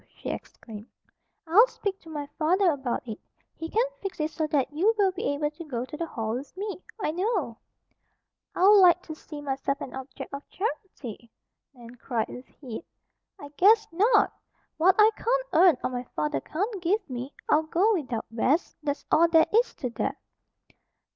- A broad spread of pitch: Yes, wide, 6.6 semitones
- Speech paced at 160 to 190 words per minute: Yes, average, 180 wpm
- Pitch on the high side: Yes, very high, 315 Hz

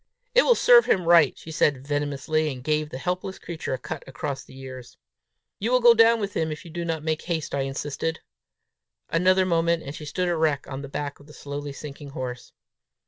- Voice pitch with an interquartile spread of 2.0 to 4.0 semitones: Yes, average, 3.6 semitones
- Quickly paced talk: Yes, fast, 210 wpm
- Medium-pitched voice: Yes, medium, 155 Hz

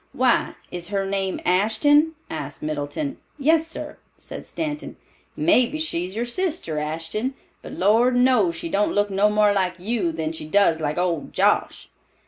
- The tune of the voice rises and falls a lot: Yes, wide, 7.1 semitones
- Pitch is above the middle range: Yes, high, 205 Hz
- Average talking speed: Yes, average, 155 wpm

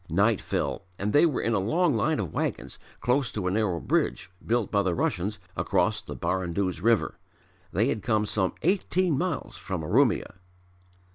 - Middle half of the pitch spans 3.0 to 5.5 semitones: Yes, average, 4.7 semitones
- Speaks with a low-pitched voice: Yes, low, 105 Hz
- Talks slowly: No, average, 170 wpm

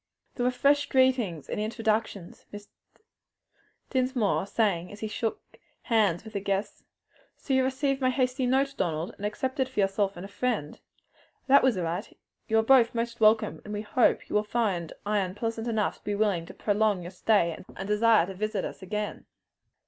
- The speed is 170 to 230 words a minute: Yes, average, 180 wpm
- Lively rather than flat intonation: No, average, 3.9 semitones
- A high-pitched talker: Yes, high, 215 Hz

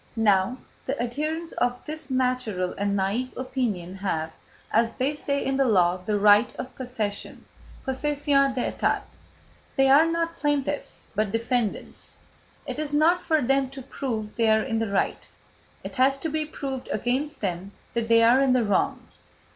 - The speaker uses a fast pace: No, average, 165 wpm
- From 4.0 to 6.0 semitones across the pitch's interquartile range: Yes, average, 4.4 semitones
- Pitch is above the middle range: Yes, very high, 250 Hz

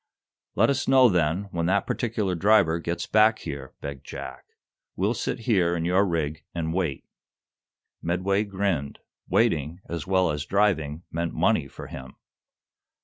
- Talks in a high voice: No, very low, 85 Hz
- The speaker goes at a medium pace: Yes, average, 145 wpm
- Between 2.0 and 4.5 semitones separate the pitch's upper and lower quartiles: Yes, average, 3.9 semitones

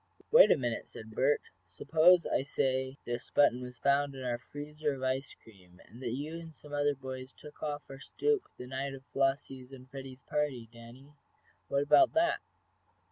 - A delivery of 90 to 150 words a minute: No, average, 185 wpm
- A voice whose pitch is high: No, low, 135 Hz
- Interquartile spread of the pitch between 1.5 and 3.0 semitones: Yes, narrow, 2.4 semitones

